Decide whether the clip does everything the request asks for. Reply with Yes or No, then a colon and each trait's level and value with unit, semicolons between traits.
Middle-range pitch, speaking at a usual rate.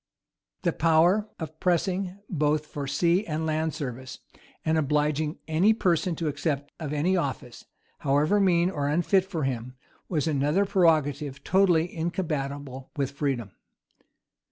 No: medium, 155 Hz; slow, 130 wpm